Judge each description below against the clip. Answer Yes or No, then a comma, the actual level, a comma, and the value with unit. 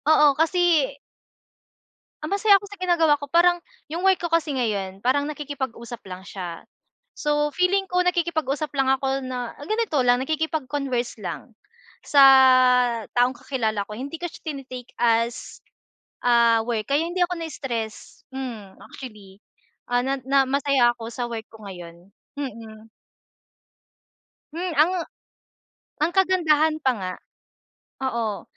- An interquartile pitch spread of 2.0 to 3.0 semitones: No, wide, 5.5 semitones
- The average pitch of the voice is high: Yes, very high, 270 Hz